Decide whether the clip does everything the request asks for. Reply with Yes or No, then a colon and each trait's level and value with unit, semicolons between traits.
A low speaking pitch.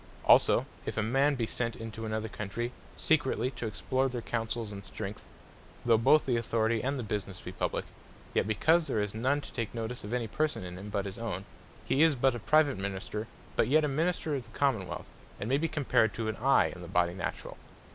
Yes: low, 115 Hz